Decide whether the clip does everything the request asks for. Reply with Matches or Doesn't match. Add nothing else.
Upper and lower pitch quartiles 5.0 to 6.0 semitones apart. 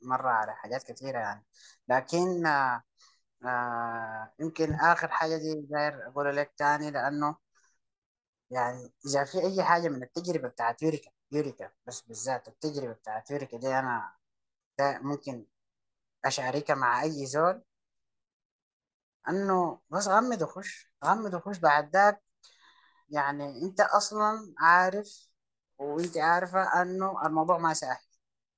Doesn't match